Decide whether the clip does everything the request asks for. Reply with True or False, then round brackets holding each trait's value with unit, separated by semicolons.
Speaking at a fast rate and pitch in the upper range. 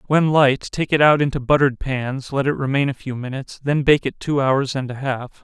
False (245 wpm; 135 Hz)